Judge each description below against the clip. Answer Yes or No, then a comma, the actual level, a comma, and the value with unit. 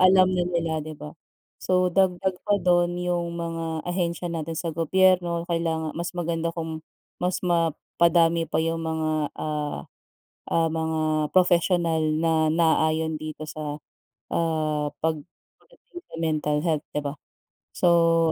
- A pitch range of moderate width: No, narrow, 1.7 semitones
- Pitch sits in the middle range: Yes, medium, 165 Hz